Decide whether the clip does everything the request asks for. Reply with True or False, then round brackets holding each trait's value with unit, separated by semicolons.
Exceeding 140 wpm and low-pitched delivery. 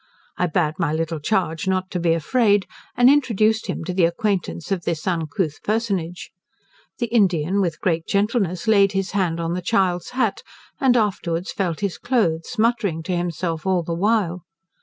False (170 wpm; 185 Hz)